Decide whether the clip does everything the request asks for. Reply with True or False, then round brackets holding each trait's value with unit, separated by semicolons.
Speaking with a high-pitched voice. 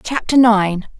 True (220 Hz)